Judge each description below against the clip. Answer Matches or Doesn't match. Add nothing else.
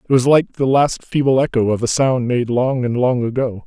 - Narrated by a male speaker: Matches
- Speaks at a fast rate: Matches